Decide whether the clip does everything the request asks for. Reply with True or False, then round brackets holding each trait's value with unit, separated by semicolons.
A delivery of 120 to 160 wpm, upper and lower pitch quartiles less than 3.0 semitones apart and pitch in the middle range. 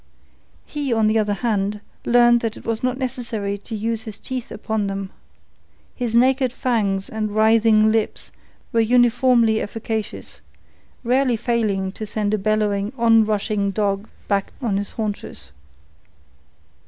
False (140 wpm; 2.4 semitones; 220 Hz)